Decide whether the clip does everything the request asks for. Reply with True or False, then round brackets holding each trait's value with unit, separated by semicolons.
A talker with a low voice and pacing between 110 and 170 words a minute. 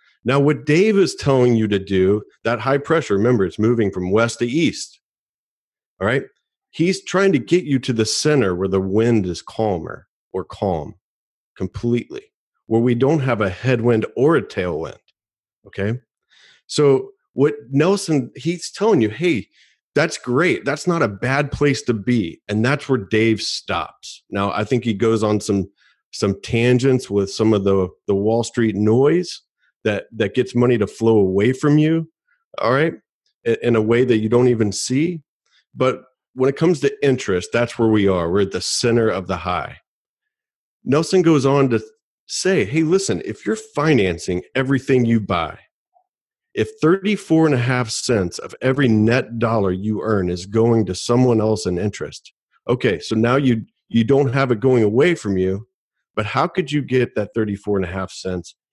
False (120 Hz; 180 wpm)